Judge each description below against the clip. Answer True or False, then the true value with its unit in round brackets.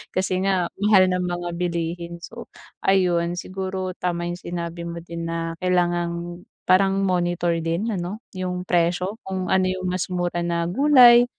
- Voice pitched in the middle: True (180 Hz)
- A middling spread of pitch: False (1.5 semitones)